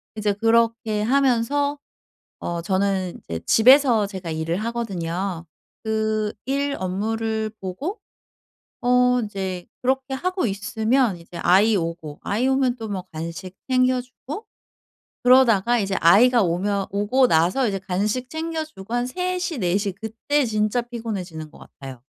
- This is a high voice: Yes, high, 220 Hz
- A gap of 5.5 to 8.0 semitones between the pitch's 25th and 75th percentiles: No, average, 5.1 semitones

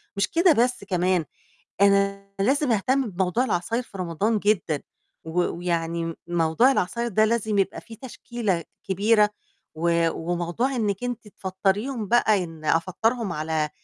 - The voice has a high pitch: Yes, high, 200 Hz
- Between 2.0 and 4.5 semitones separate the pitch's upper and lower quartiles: No, average, 5.0 semitones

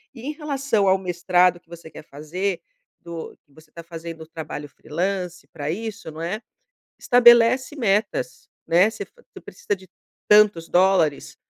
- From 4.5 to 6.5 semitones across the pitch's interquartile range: Yes, average, 4.8 semitones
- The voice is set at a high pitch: No, medium, 180 Hz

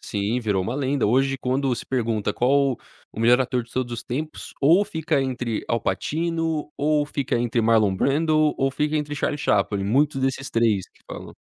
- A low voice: Yes, low, 130 Hz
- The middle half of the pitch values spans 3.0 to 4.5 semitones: Yes, average, 4.2 semitones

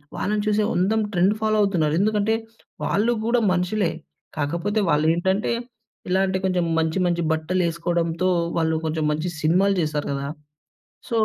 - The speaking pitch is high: No, medium, 180 Hz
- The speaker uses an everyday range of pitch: Yes, average, 4.1 semitones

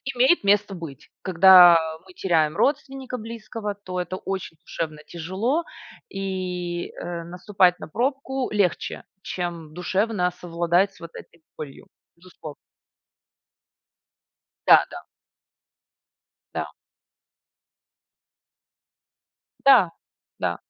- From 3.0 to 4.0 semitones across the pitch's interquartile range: Yes, average, 3.5 semitones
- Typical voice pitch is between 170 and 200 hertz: Yes, medium, 185 Hz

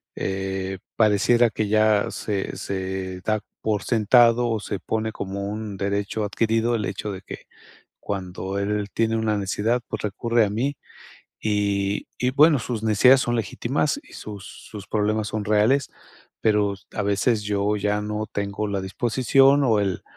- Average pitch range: No, narrow, 2.1 semitones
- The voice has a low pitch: Yes, low, 105 Hz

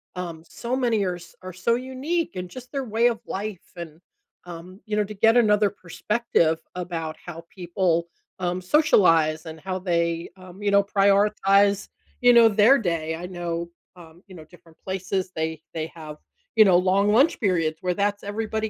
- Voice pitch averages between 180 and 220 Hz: Yes, medium, 185 Hz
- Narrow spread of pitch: No, average, 3.8 semitones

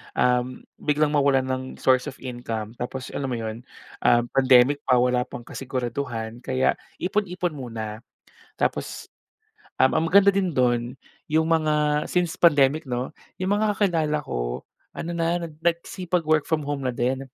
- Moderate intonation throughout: Yes, average, 4.6 semitones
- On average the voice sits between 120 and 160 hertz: Yes, low, 135 Hz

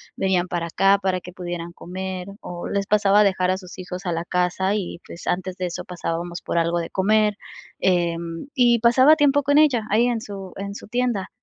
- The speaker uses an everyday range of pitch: Yes, average, 3.2 semitones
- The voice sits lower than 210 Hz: Yes, high, 190 Hz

